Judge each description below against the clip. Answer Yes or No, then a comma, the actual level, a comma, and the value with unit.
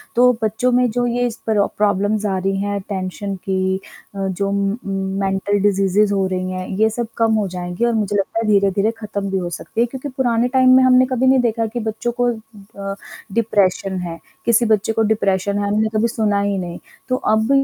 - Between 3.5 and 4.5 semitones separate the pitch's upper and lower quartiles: No, average, 3.1 semitones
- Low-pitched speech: No, high, 205 Hz